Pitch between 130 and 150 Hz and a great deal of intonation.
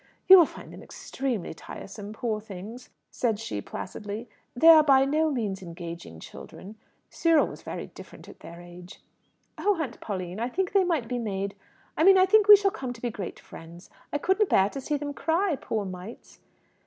No: high, 235 Hz; wide, 8.5 semitones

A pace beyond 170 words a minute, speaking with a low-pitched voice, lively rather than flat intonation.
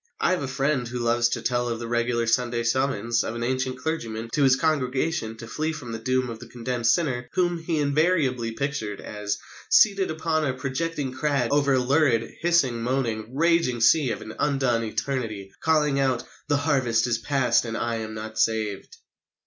No: average, 190 wpm; low, 125 Hz; average, 3.9 semitones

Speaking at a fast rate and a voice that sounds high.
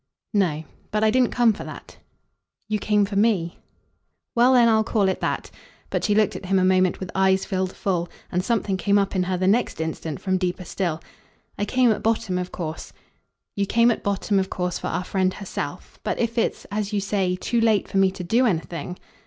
Yes: fast, 215 wpm; high, 195 Hz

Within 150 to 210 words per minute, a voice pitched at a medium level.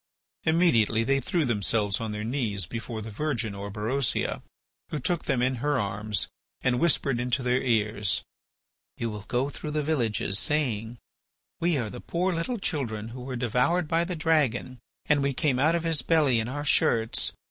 No: average, 175 wpm; low, 125 Hz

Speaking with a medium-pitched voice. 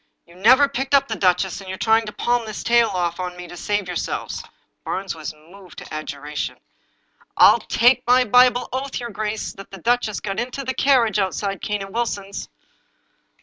No: high, 210 Hz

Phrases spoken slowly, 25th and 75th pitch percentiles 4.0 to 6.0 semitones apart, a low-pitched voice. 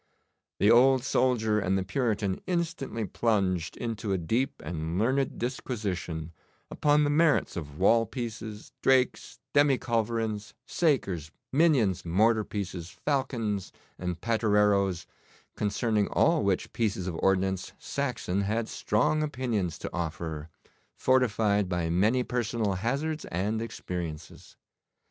Yes: slow, 115 wpm; average, 5.2 semitones; low, 110 Hz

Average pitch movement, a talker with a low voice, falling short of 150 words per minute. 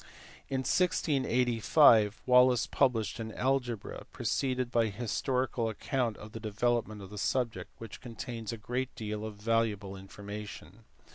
Yes: average, 3.0 semitones; low, 115 Hz; average, 140 wpm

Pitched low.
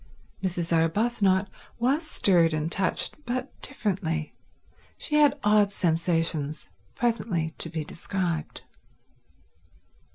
No: medium, 185 Hz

